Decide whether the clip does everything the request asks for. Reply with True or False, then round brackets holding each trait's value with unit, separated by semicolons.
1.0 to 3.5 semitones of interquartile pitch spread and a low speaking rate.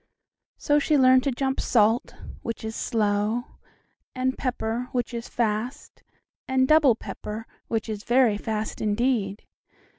True (3.1 semitones; 130 wpm)